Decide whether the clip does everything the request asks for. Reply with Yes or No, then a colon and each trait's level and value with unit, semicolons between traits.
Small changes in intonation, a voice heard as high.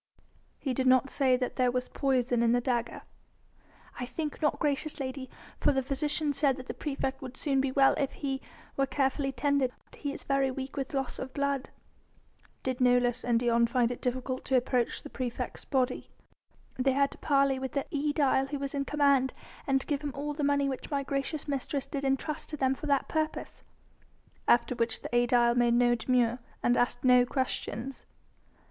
Yes: narrow, 2.0 semitones; very high, 265 Hz